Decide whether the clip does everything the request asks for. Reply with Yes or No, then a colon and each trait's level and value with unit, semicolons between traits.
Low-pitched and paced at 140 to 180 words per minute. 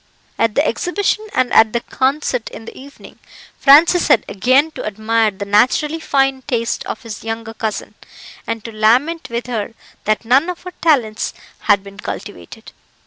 No: high, 235 Hz; average, 165 wpm